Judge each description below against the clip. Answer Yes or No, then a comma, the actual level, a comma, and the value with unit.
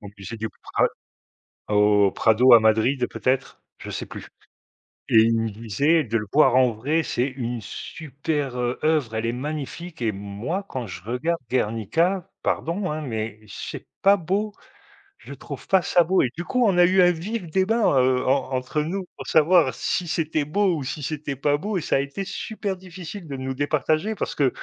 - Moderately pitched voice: Yes, medium, 145 Hz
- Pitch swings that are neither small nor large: No, wide, 6.6 semitones